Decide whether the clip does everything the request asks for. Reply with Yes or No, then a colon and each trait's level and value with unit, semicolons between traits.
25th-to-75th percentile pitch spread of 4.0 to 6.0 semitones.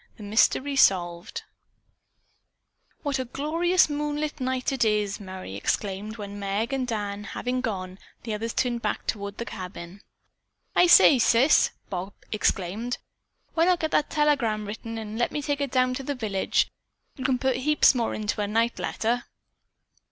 Yes: average, 4.8 semitones